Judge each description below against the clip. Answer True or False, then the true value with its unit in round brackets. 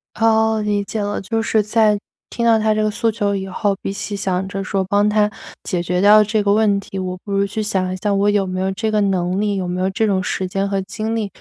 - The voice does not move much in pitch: True (1.9 semitones)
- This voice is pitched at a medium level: False (205 Hz)